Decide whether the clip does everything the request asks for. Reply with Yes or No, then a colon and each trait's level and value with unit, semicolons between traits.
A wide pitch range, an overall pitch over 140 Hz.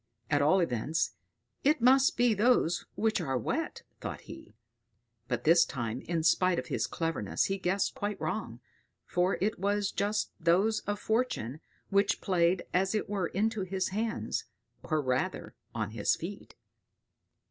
No: average, 4.7 semitones; medium, 185 Hz